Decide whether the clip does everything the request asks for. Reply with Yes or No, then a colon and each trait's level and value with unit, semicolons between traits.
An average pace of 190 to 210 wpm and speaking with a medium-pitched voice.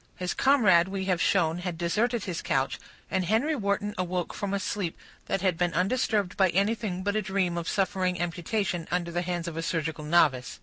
Yes: average, 200 wpm; medium, 180 Hz